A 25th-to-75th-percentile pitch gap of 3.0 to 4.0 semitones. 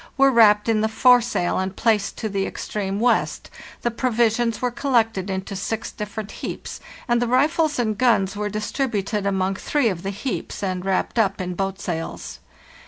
Yes: average, 3.6 semitones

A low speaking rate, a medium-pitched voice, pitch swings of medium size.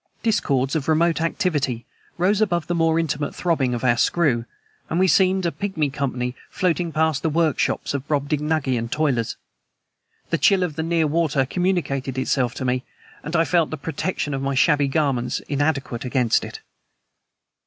No: average, 165 wpm; medium, 150 Hz; average, 3.9 semitones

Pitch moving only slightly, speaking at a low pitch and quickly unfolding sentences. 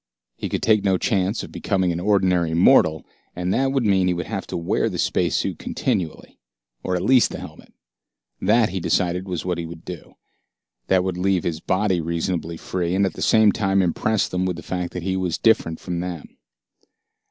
Yes: narrow, 2.1 semitones; very low, 90 Hz; fast, 210 wpm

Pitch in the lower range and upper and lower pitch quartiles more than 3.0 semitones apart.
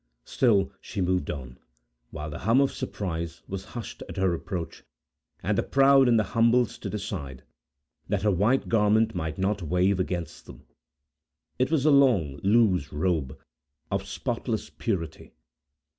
Yes: low, 100 Hz; average, 5.2 semitones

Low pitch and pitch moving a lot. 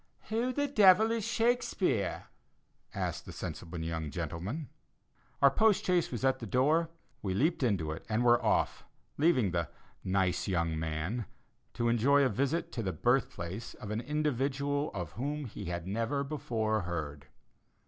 Yes: low, 120 Hz; wide, 8.3 semitones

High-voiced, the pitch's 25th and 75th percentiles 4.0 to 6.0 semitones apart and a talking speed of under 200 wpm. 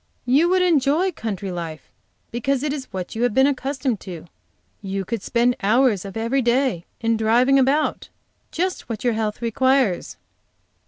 Yes: high, 240 Hz; average, 4.3 semitones; average, 160 wpm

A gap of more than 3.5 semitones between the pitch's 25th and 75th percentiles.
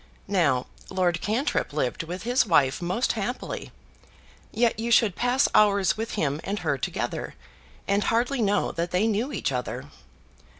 Yes: average, 5.1 semitones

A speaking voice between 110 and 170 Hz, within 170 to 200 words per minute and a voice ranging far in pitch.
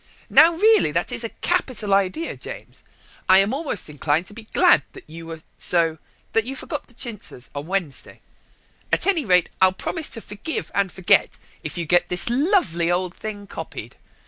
No: high, 195 Hz; average, 180 wpm; wide, 6.9 semitones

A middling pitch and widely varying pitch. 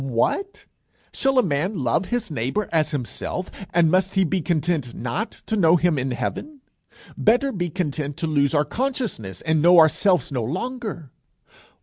Yes: medium, 170 Hz; wide, 5.9 semitones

